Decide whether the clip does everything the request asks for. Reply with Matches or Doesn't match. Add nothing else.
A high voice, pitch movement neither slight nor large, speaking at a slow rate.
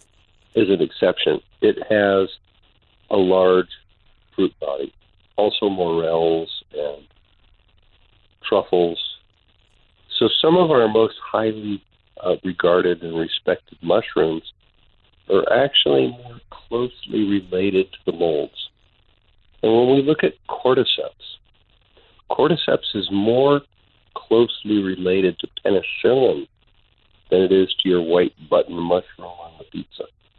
Doesn't match